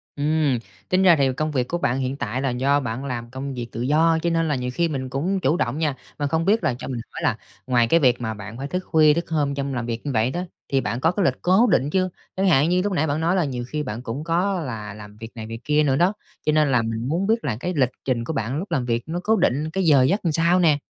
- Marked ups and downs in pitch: No, average, 5.0 semitones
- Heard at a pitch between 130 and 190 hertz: Yes, medium, 140 Hz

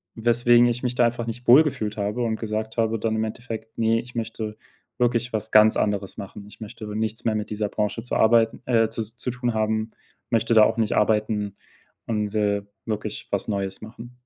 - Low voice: Yes, low, 110 Hz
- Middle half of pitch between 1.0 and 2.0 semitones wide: Yes, narrow, 1.7 semitones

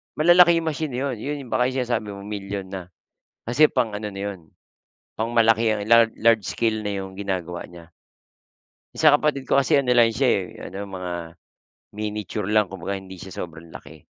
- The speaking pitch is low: Yes, low, 105 Hz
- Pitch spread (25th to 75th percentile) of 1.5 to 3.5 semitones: No, average, 4.4 semitones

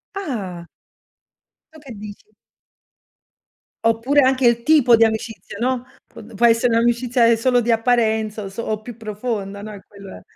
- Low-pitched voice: No, high, 230 Hz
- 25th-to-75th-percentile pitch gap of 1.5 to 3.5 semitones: Yes, narrow, 2.5 semitones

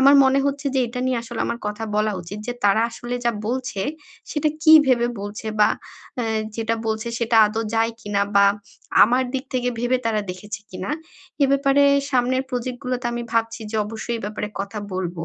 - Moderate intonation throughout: Yes, average, 3.2 semitones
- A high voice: Yes, high, 230 Hz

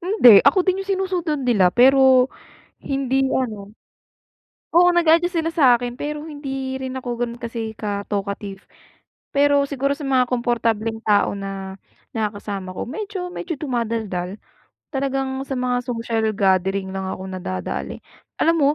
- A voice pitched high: Yes, very high, 250 Hz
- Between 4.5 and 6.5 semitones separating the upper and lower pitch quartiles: Yes, wide, 5.4 semitones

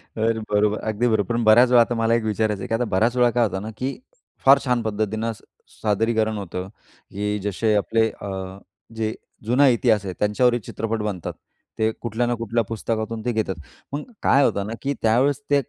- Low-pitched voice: Yes, low, 110 Hz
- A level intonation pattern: Yes, narrow, 2.1 semitones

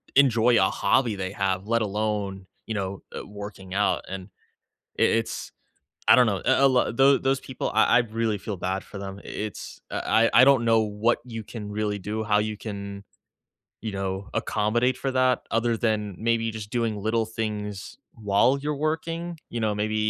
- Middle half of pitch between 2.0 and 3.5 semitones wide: Yes, narrow, 2.5 semitones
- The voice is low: Yes, low, 110 Hz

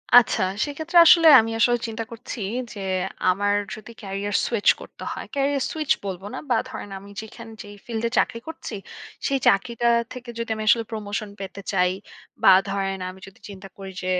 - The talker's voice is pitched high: Yes, high, 220 Hz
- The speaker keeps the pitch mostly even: No, average, 3.5 semitones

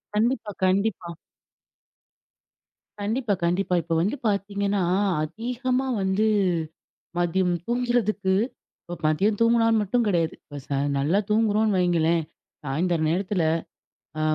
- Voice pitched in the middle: No, high, 200 Hz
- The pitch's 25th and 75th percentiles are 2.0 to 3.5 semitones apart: No, average, 4.1 semitones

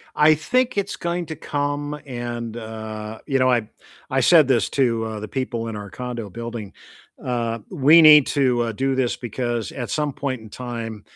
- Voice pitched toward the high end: No, low, 125 Hz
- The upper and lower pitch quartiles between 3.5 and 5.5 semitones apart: Yes, average, 4.0 semitones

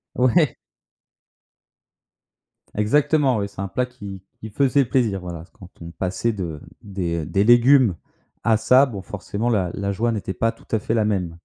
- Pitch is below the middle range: Yes, low, 105 Hz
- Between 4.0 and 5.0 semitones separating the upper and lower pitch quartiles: Yes, average, 4.4 semitones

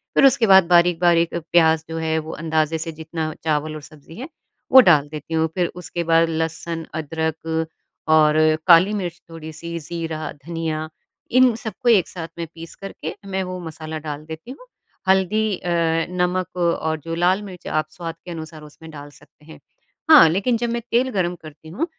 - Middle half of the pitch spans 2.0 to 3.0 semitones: Yes, narrow, 2.4 semitones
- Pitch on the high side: No, medium, 165 Hz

